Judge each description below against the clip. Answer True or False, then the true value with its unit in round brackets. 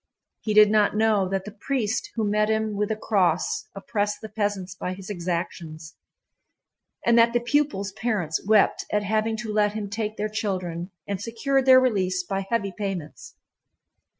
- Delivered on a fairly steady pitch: True (2.3 semitones)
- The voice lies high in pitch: True (210 Hz)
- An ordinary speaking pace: True (170 wpm)